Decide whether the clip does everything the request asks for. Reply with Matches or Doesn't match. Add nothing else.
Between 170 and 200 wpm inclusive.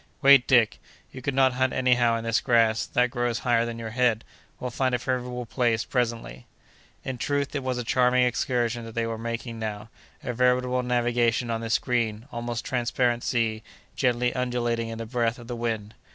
Matches